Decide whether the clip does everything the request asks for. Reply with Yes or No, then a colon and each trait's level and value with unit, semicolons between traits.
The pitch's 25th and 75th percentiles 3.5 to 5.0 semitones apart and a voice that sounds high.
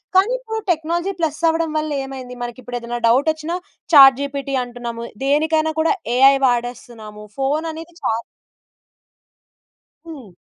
Yes: average, 4.6 semitones; very high, 280 Hz